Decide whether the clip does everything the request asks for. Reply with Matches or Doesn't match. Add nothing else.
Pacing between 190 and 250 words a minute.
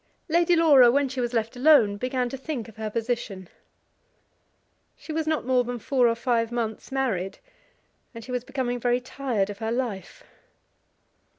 Doesn't match